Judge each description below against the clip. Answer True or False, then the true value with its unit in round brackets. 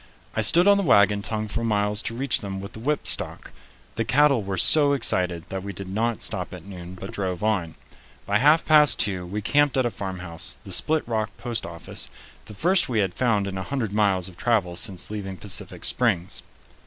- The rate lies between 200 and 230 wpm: True (205 wpm)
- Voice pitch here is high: False (105 Hz)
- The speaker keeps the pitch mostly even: False (4.1 semitones)